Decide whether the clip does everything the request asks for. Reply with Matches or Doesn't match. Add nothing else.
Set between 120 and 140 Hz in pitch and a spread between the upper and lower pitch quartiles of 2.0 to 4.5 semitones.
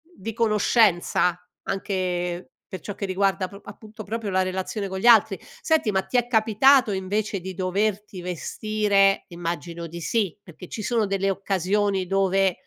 Doesn't match